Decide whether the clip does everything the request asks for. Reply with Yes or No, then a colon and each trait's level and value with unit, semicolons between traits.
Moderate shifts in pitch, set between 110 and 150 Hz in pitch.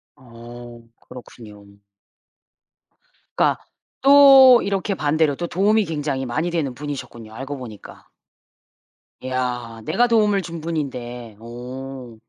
No: wide, 6.0 semitones; low, 135 Hz